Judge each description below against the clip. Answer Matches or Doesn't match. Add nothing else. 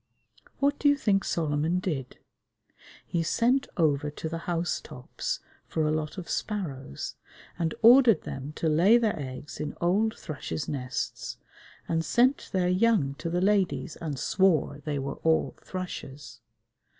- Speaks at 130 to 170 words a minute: Matches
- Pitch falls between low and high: Matches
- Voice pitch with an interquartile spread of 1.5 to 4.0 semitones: Doesn't match